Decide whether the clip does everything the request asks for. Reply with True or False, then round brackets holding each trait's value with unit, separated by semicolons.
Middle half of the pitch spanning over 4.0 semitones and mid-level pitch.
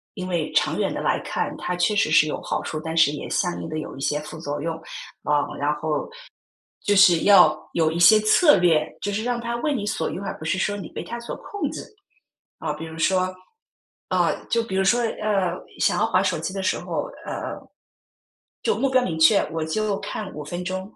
True (4.9 semitones; 180 Hz)